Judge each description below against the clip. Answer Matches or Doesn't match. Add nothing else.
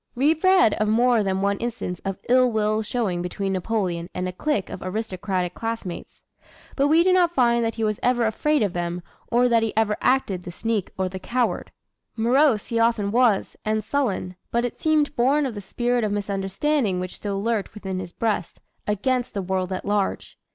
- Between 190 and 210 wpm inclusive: Matches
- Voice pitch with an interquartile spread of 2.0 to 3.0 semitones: Doesn't match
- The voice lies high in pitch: Matches